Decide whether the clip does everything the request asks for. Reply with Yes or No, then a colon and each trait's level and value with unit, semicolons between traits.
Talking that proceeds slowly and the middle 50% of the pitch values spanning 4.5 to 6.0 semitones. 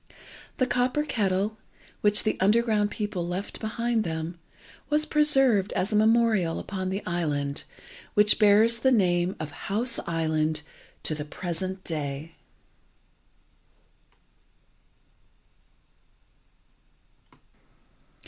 Yes: slow, 95 wpm; average, 5.1 semitones